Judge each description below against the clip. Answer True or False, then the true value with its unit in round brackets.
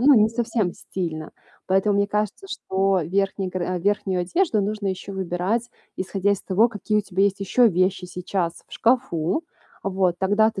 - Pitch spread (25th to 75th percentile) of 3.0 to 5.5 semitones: False (2.6 semitones)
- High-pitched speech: True (195 Hz)